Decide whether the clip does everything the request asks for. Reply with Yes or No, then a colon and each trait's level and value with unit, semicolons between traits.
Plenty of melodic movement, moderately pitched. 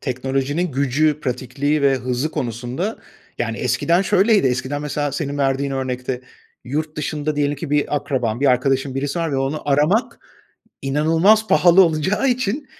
No: average, 3.2 semitones; medium, 145 Hz